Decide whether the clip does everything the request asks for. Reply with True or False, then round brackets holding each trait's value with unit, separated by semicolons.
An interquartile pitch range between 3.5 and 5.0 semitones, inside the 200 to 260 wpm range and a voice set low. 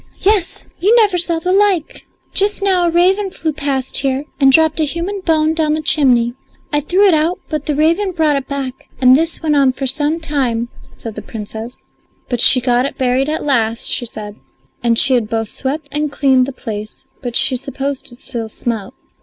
False (4.6 semitones; 205 wpm; 280 Hz)